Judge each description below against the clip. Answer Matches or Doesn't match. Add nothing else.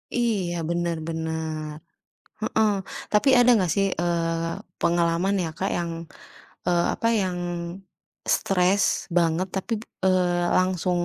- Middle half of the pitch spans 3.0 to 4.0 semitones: Doesn't match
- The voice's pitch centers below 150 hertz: Doesn't match